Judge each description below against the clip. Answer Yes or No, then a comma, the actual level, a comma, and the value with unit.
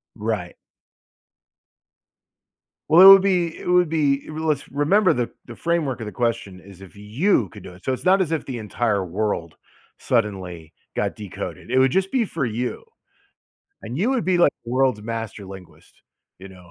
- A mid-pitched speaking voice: No, low, 120 Hz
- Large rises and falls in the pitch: Yes, wide, 8.2 semitones